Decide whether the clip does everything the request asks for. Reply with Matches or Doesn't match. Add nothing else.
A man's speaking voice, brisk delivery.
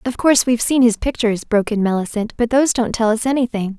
Doesn't match